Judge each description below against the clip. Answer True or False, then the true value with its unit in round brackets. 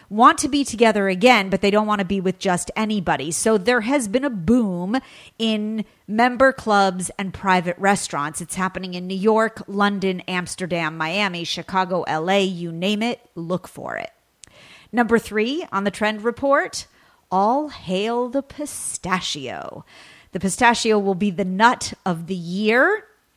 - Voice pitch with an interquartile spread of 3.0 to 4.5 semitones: True (4.0 semitones)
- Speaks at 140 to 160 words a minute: True (155 wpm)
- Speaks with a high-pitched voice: True (205 Hz)